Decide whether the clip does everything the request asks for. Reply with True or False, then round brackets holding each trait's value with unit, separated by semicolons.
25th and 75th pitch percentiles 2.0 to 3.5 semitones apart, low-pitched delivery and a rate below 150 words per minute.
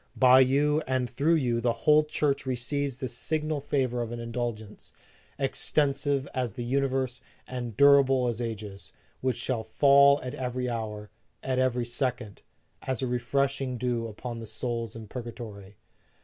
False (2.7 semitones; 125 Hz; 155 wpm)